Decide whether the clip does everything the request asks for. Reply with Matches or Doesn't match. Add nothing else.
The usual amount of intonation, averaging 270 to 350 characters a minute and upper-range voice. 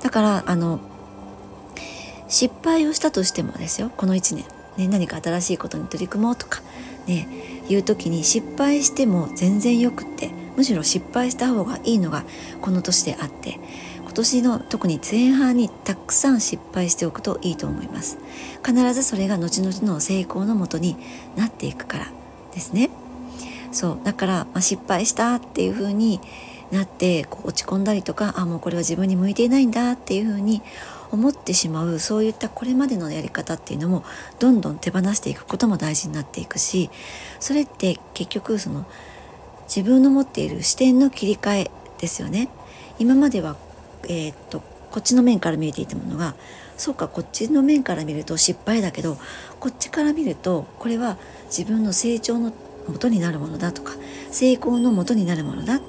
Doesn't match